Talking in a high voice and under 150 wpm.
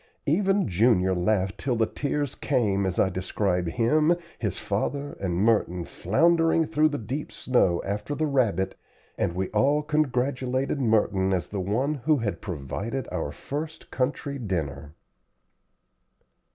No: low, 115 Hz; average, 140 wpm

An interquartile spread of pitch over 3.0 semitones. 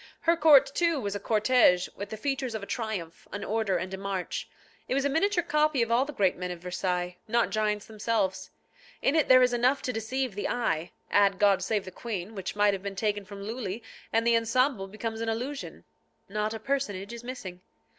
Yes: average, 4.4 semitones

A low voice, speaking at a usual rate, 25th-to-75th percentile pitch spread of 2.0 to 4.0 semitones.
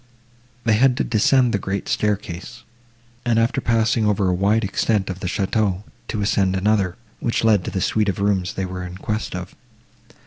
Yes: low, 105 Hz; average, 185 wpm; average, 2.8 semitones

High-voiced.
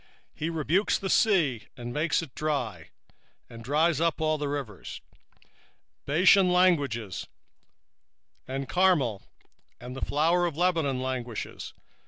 No: medium, 150 Hz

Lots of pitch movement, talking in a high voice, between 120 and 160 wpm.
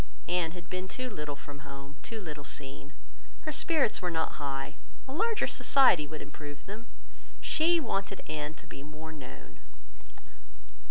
No: wide, 6.9 semitones; medium, 160 Hz; average, 155 wpm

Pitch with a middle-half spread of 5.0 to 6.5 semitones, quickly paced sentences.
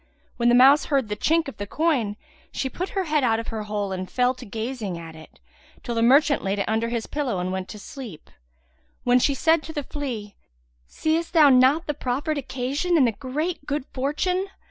Yes: wide, 5.4 semitones; fast, 210 wpm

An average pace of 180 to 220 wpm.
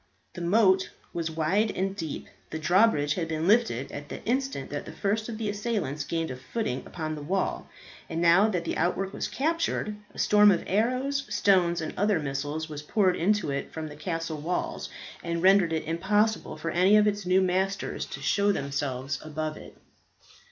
Yes: average, 185 wpm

